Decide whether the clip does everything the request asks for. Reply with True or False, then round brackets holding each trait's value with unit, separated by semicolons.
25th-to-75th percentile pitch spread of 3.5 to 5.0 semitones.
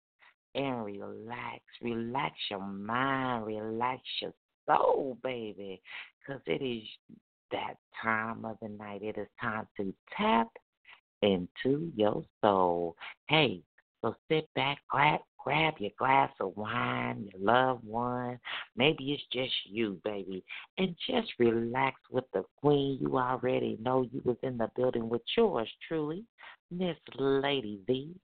True (3.9 semitones)